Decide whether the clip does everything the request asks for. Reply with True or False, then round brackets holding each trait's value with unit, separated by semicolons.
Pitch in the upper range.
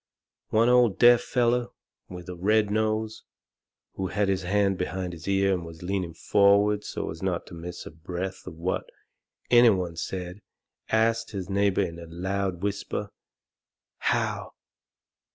False (95 Hz)